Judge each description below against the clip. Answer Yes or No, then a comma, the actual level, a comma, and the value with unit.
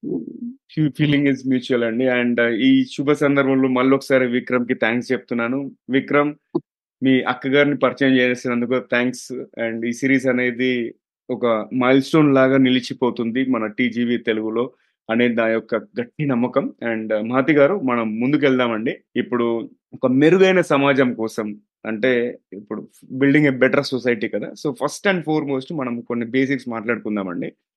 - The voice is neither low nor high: No, low, 130 Hz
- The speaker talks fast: Yes, fast, 140 wpm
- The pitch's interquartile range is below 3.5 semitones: Yes, narrow, 2.5 semitones